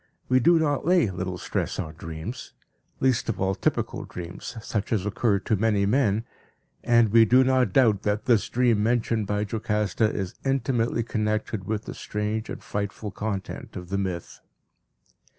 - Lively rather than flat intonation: No, average, 3.1 semitones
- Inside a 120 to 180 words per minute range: Yes, average, 165 wpm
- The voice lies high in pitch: No, low, 110 Hz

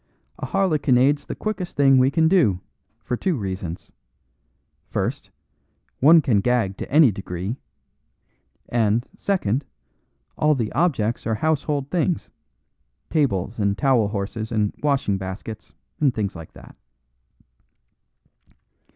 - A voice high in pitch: No, low, 125 Hz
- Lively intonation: Yes, wide, 6.6 semitones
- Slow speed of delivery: Yes, slow, 115 wpm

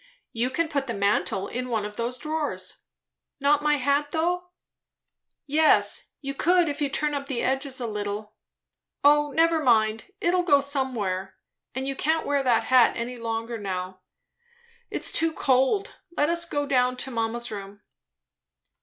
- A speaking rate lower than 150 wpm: No, average, 160 wpm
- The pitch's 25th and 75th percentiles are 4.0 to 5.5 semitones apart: Yes, average, 4.5 semitones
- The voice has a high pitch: Yes, very high, 265 Hz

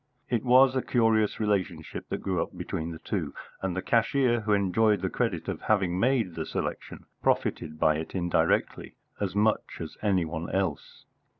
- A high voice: No, very low, 95 Hz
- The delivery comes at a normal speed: Yes, average, 175 wpm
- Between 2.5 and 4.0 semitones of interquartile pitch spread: No, average, 4.4 semitones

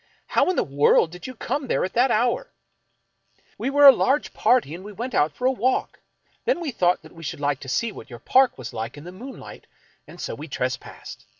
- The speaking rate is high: Yes, fast, 235 wpm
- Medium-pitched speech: No, high, 225 Hz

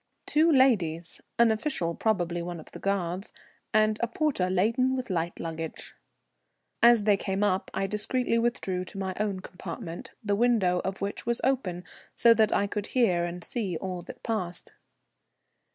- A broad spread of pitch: No, average, 4.5 semitones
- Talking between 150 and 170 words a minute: Yes, average, 165 wpm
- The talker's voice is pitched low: No, high, 200 Hz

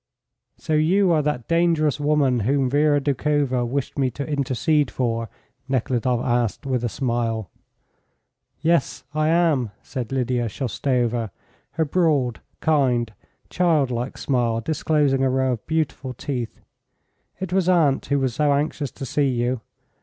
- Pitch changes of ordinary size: Yes, average, 3.7 semitones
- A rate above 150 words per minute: No, average, 140 wpm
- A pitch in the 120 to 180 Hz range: Yes, low, 135 Hz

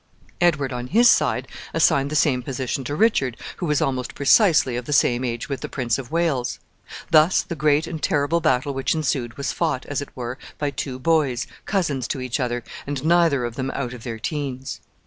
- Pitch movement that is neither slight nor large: Yes, average, 3.4 semitones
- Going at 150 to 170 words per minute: No, fast, 205 wpm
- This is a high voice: No, medium, 140 Hz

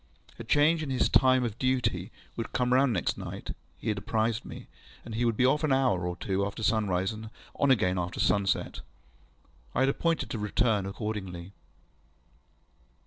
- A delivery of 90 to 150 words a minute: No, average, 180 wpm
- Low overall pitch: Yes, low, 110 Hz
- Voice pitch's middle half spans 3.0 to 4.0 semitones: No, average, 4.5 semitones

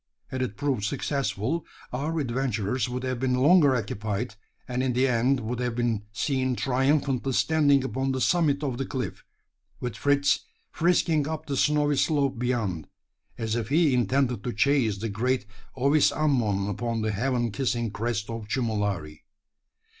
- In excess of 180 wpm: No, average, 155 wpm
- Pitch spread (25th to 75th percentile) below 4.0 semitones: Yes, average, 3.5 semitones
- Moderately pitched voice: No, low, 125 Hz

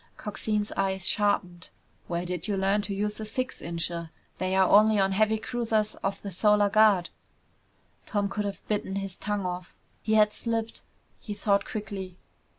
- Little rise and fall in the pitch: Yes, narrow, 1.9 semitones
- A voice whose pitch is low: No, high, 205 Hz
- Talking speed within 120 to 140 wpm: No, average, 160 wpm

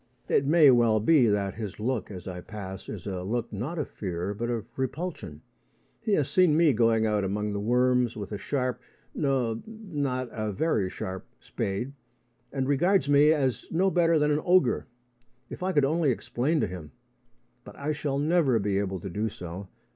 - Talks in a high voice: No, low, 125 Hz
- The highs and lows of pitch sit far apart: Yes, wide, 6.4 semitones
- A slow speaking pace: No, average, 185 wpm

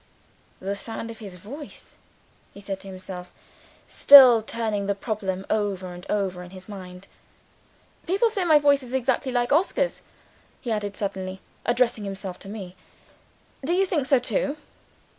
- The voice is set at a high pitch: Yes, high, 210 Hz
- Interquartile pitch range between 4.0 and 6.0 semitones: Yes, average, 5.3 semitones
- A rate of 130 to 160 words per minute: Yes, average, 155 wpm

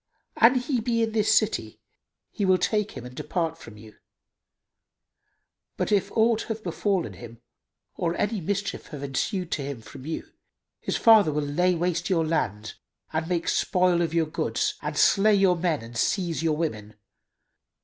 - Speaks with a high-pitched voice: No, medium, 175 Hz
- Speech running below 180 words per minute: Yes, average, 170 wpm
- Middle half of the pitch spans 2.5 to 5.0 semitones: No, wide, 5.4 semitones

